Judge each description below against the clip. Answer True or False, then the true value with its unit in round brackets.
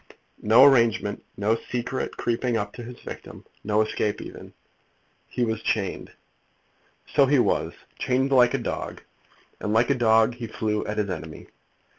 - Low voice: True (115 Hz)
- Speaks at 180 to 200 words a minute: False (155 wpm)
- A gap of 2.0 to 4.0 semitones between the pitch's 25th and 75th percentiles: True (2.7 semitones)